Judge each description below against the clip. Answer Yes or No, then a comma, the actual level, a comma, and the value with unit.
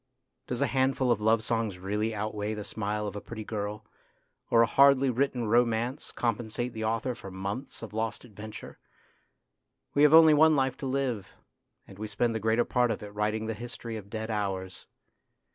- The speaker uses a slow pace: No, average, 185 wpm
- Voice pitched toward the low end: Yes, low, 110 Hz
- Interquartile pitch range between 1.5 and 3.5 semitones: Yes, average, 2.8 semitones